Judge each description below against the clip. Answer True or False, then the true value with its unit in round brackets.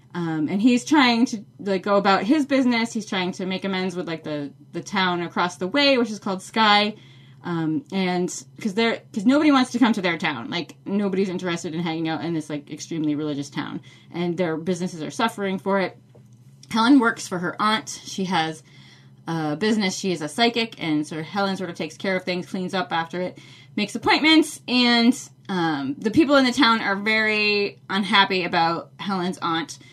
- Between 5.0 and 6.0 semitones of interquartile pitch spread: True (5.4 semitones)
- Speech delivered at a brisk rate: False (195 wpm)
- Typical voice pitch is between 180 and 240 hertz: True (185 Hz)